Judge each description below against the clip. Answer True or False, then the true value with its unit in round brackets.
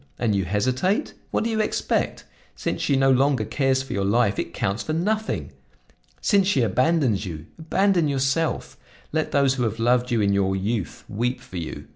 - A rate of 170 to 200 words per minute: True (185 wpm)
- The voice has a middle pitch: False (125 Hz)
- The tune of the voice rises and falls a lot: True (7.1 semitones)